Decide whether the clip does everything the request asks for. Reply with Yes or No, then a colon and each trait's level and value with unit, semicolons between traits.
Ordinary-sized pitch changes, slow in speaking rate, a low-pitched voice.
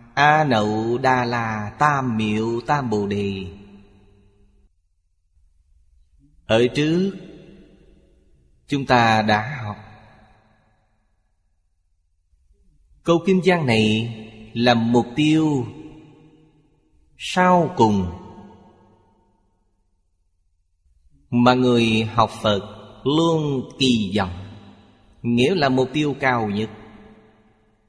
Yes: average, 4.5 semitones; slow, 80 wpm; low, 110 Hz